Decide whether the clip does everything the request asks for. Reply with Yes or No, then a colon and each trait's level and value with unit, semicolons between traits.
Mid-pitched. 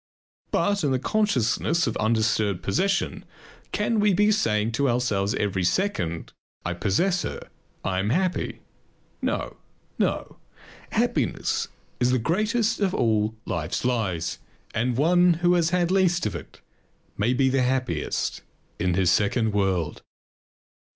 No: low, 125 Hz